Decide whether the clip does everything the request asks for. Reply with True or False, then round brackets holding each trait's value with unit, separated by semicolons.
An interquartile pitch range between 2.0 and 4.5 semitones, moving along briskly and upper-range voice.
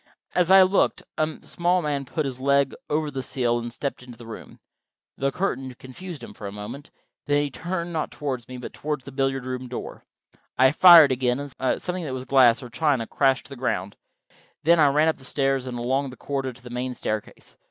False (3.1 semitones; 215 wpm; 135 Hz)